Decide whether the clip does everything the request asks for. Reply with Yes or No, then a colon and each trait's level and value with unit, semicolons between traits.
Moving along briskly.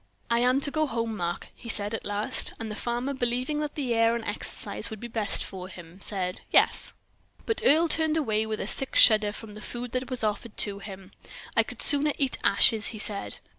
Yes: fast, 210 wpm